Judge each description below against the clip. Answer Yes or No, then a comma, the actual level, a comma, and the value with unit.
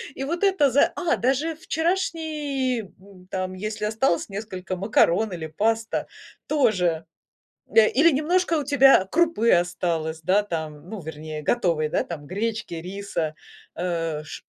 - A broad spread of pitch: Yes, wide, 8.0 semitones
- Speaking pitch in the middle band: No, high, 205 Hz